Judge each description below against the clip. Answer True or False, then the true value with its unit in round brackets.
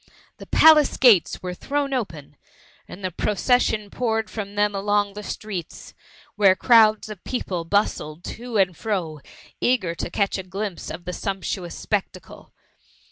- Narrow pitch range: False (3.3 semitones)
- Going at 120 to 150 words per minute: True (145 wpm)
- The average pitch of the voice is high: True (205 Hz)